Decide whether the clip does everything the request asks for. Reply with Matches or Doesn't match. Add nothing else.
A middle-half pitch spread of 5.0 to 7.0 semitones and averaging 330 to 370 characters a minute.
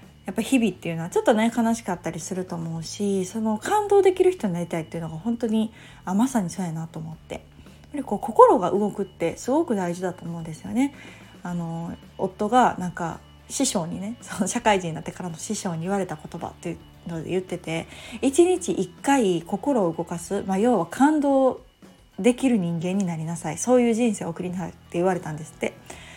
Matches